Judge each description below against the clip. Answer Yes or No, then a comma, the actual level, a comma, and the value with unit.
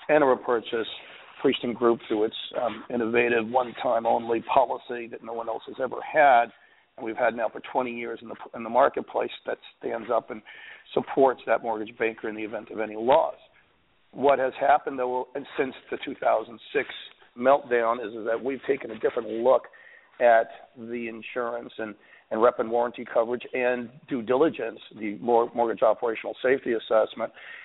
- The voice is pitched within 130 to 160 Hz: No, low, 120 Hz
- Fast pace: No, average, 165 wpm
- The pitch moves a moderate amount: No, narrow, 1.7 semitones